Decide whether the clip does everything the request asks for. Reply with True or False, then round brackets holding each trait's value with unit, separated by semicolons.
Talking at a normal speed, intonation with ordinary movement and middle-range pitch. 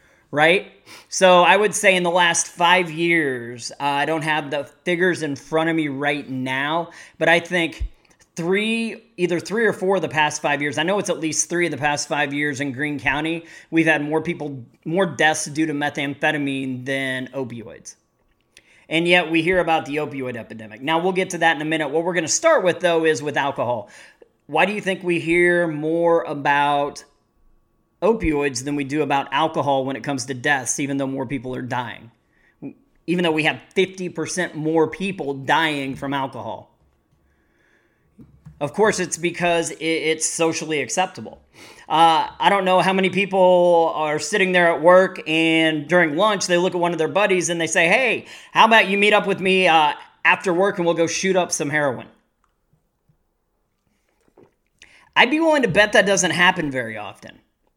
True (190 wpm; 3.7 semitones; 160 Hz)